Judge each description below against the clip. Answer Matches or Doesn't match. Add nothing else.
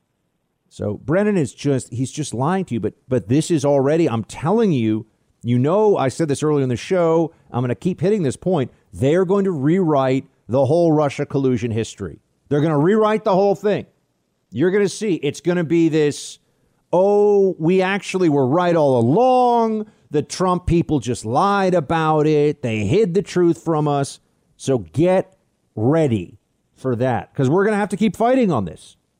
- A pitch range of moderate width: Doesn't match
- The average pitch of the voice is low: Doesn't match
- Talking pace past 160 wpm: Matches